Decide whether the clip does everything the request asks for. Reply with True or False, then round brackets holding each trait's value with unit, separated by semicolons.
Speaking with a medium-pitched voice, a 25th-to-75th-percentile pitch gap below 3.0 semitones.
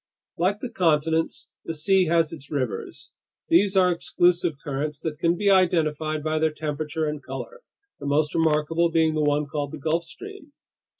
True (160 Hz; 2.4 semitones)